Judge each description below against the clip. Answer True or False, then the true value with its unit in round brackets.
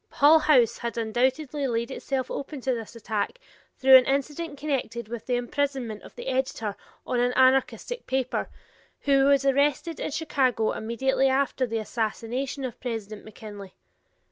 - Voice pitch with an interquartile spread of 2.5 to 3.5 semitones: True (3.2 semitones)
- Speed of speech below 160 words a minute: True (150 wpm)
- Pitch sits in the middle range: False (260 Hz)